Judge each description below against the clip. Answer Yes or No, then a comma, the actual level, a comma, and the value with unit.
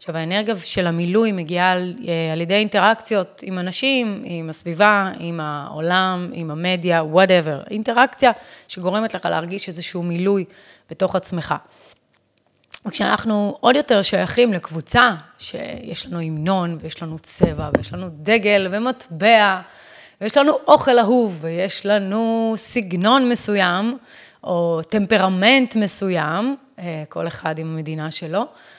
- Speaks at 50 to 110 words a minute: No, average, 120 wpm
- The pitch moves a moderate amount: Yes, average, 4.5 semitones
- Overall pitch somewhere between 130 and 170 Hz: No, high, 190 Hz